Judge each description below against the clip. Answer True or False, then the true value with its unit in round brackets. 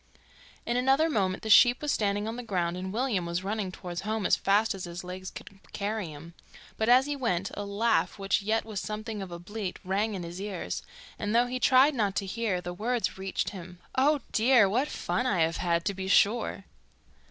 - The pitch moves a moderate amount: True (3.8 semitones)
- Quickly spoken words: True (215 wpm)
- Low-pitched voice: False (205 Hz)